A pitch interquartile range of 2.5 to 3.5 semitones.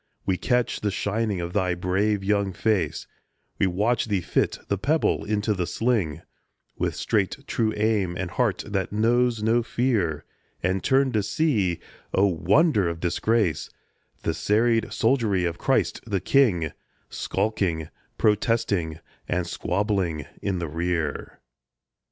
No: average, 4.1 semitones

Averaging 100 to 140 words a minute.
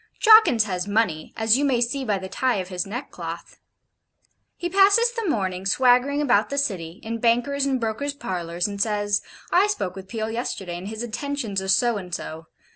No: average, 190 wpm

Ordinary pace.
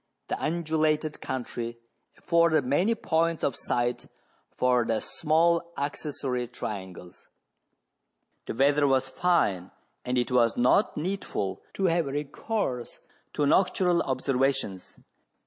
No: slow, 115 wpm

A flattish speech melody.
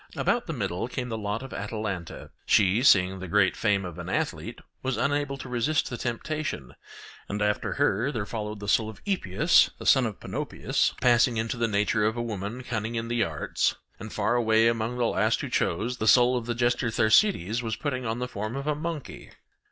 No: average, 3.3 semitones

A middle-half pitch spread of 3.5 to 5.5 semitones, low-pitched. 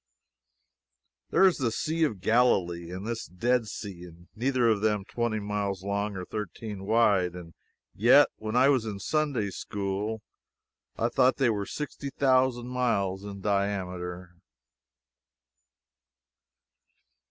Yes: average, 4.0 semitones; low, 105 Hz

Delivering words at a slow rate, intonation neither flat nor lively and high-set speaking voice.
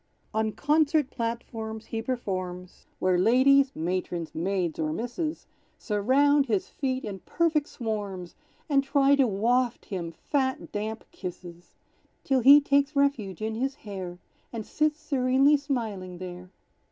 No: slow, 130 wpm; wide, 6.7 semitones; high, 230 Hz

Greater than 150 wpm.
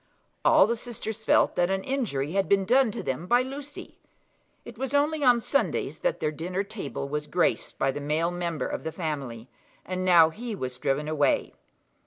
Yes: average, 190 wpm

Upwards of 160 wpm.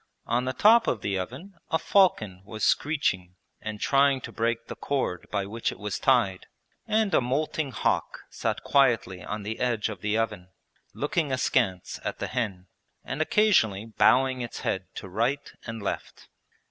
Yes: average, 170 wpm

